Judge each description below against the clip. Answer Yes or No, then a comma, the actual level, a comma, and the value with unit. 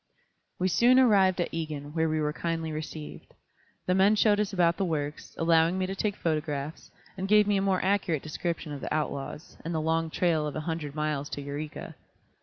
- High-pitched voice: No, medium, 165 Hz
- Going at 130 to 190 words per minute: No, fast, 205 wpm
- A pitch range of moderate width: Yes, average, 3.6 semitones